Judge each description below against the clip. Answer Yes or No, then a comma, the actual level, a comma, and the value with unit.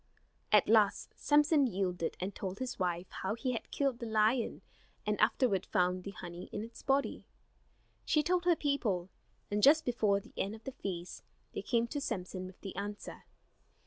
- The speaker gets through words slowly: No, average, 175 wpm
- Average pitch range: No, wide, 5.8 semitones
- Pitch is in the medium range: No, high, 215 Hz